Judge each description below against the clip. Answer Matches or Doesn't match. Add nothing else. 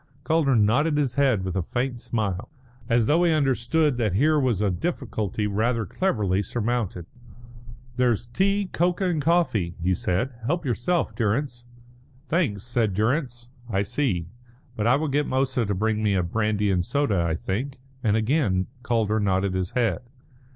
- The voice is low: Matches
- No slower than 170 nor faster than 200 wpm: Doesn't match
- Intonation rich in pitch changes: Matches